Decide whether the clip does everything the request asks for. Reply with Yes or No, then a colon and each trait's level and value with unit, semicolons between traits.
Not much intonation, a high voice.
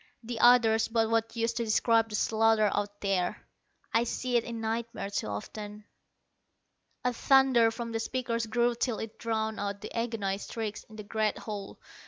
Yes: narrow, 1.7 semitones; high, 225 Hz